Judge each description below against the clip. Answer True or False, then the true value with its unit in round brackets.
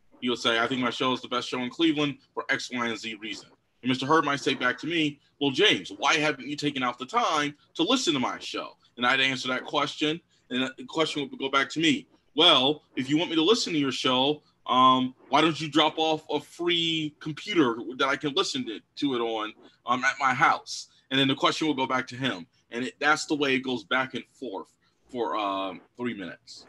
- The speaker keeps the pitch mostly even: False (3.6 semitones)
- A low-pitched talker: False (145 Hz)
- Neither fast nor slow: False (245 wpm)